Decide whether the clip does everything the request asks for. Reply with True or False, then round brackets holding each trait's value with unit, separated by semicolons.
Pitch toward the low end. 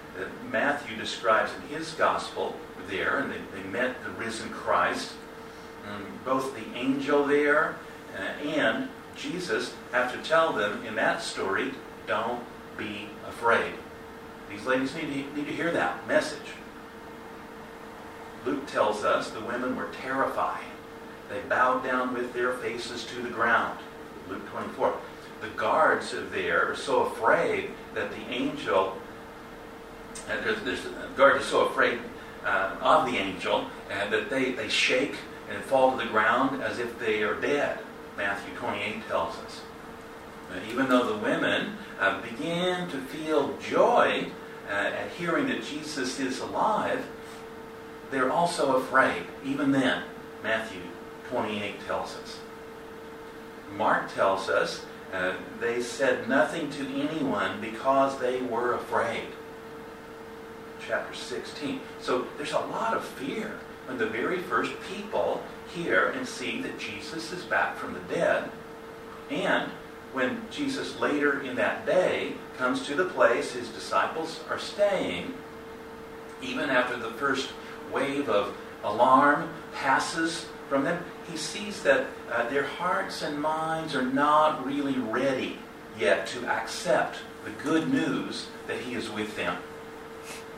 False (155 Hz)